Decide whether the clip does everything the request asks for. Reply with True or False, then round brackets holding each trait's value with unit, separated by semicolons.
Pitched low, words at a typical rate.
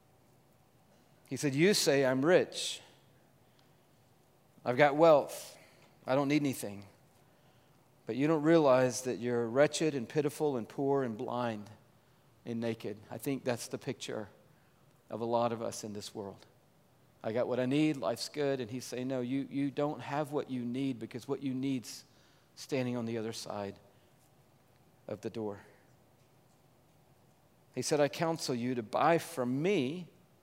True (130 Hz; 160 wpm)